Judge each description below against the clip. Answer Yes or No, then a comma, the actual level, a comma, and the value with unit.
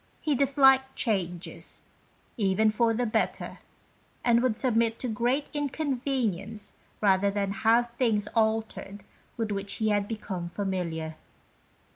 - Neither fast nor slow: No, slow, 120 wpm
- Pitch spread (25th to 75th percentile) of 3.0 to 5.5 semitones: Yes, average, 3.6 semitones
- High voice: Yes, high, 220 Hz